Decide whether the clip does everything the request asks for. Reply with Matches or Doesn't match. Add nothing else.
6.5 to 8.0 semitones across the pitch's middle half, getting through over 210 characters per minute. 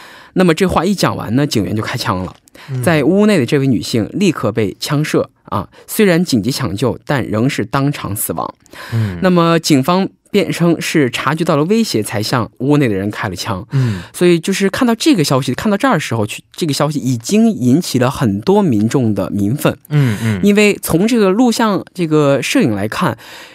Matches